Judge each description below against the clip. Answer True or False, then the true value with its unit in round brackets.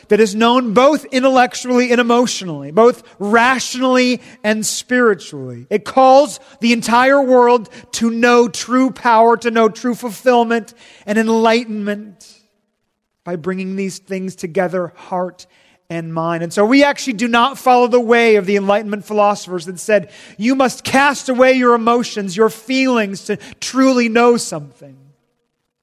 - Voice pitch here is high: True (225 Hz)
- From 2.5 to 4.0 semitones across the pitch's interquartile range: True (3.7 semitones)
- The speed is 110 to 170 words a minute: True (140 wpm)